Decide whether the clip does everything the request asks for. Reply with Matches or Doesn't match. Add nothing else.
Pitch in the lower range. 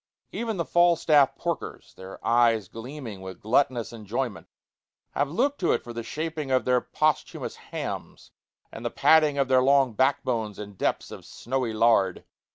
Matches